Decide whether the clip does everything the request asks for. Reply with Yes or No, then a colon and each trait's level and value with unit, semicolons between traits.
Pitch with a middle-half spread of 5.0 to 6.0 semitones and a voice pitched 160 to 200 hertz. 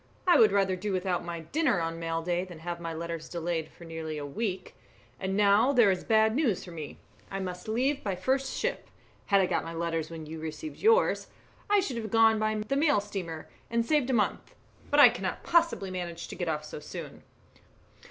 Yes: wide, 5.4 semitones; high, 190 Hz